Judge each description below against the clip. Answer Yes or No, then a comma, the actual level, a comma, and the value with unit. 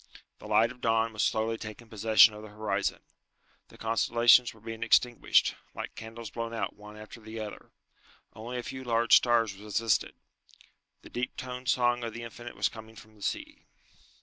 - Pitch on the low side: Yes, low, 115 Hz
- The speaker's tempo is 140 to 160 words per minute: No, average, 175 wpm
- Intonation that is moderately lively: No, narrow, 1.5 semitones